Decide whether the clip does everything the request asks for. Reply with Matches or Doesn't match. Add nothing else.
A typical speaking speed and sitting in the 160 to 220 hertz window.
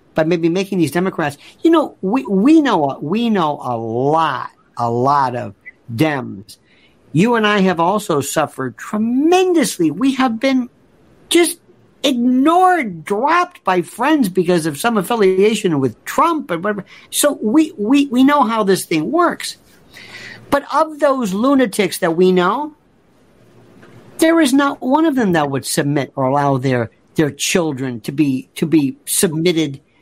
Matches